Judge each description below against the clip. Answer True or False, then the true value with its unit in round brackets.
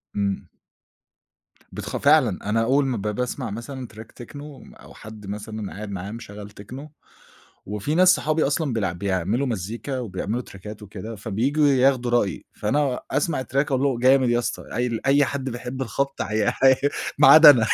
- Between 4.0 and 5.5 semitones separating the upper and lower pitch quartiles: True (4.6 semitones)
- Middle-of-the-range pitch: False (120 Hz)